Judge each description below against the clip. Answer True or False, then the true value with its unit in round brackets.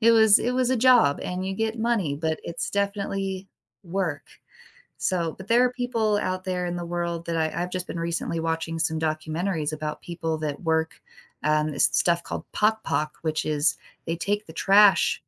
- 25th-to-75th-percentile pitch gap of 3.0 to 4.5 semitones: True (4.2 semitones)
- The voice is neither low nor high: True (175 Hz)